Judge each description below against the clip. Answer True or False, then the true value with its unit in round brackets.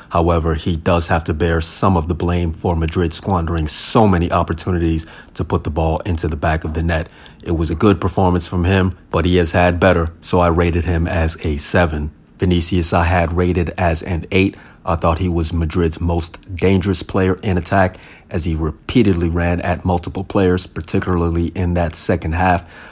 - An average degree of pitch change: False (1.8 semitones)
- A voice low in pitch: True (85 Hz)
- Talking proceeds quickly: False (195 wpm)